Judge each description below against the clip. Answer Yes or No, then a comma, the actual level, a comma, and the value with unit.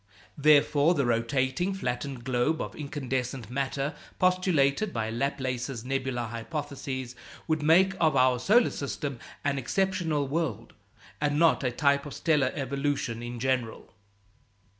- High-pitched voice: No, medium, 140 Hz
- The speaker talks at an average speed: No, slow, 125 wpm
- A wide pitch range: No, average, 3.4 semitones